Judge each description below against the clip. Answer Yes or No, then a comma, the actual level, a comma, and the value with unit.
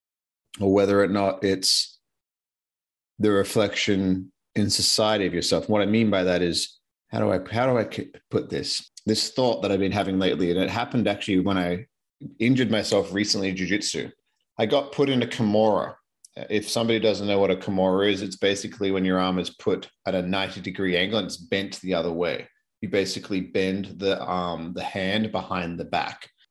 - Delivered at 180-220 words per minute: Yes, average, 190 wpm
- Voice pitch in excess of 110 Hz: No, low, 100 Hz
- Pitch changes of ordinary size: No, narrow, 2.2 semitones